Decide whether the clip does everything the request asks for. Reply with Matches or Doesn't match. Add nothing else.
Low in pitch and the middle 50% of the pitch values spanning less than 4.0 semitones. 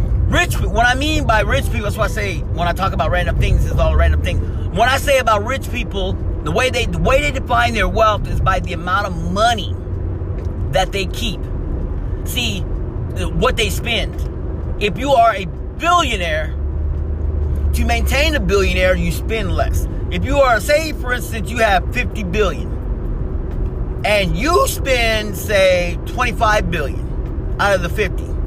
Matches